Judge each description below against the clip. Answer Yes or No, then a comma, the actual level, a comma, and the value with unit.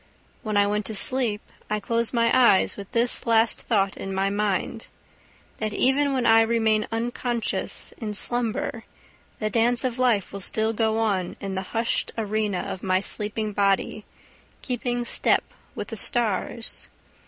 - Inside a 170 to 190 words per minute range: No, average, 155 wpm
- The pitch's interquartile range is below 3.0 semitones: Yes, narrow, 2.5 semitones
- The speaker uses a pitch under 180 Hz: No, high, 220 Hz